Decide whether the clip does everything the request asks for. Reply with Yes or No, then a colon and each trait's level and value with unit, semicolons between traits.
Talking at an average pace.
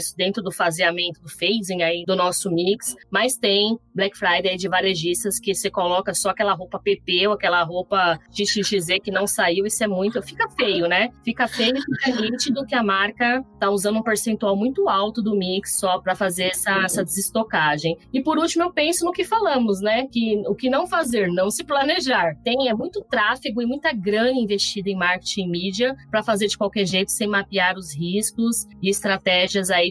No: fast, 200 wpm